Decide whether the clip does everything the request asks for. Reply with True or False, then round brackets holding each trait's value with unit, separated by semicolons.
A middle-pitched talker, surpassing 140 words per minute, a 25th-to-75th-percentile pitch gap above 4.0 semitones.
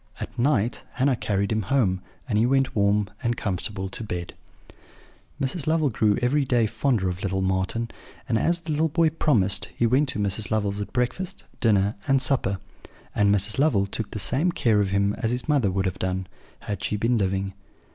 False (110 Hz; 195 wpm; 5.1 semitones)